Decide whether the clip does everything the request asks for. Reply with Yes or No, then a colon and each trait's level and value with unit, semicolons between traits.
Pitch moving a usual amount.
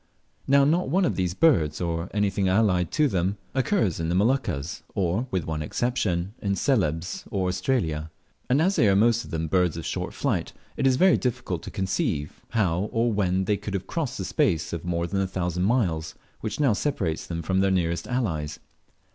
No: wide, 5.9 semitones